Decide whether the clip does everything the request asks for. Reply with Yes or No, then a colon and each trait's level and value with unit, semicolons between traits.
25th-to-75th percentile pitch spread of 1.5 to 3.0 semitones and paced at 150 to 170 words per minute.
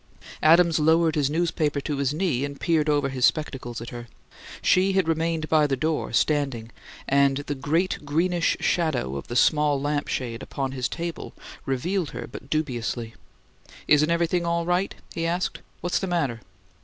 No: average, 3.7 semitones; average, 165 wpm